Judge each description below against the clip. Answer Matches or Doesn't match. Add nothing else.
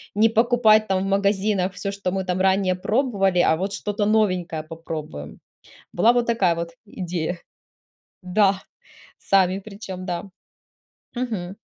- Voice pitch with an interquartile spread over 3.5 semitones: Doesn't match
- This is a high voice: Matches